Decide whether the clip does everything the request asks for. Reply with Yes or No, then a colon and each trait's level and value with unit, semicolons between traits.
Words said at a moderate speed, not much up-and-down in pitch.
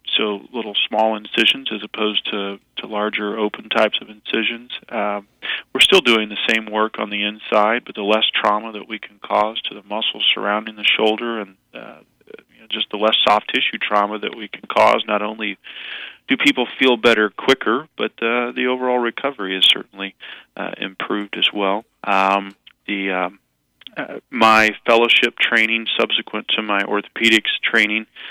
Yes: average, 170 wpm; narrow, 1.6 semitones